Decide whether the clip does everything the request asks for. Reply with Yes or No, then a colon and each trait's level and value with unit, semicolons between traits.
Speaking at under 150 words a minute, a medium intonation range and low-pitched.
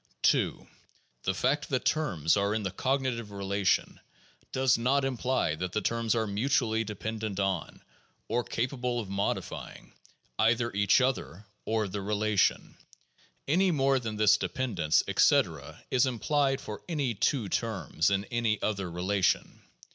Yes: average, 140 wpm; average, 4.4 semitones; low, 110 Hz